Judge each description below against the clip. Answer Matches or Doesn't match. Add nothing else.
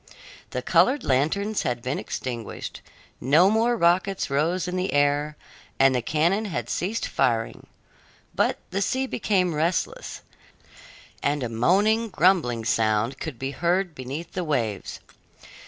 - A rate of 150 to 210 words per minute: Doesn't match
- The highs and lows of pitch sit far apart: Matches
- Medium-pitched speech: Matches